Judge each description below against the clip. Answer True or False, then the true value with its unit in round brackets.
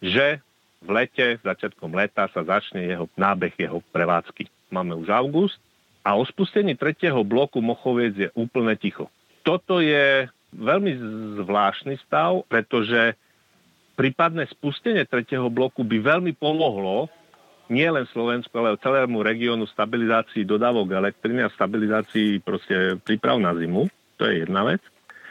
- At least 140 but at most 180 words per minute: False (130 wpm)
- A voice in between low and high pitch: False (120 Hz)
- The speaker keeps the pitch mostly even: False (5.1 semitones)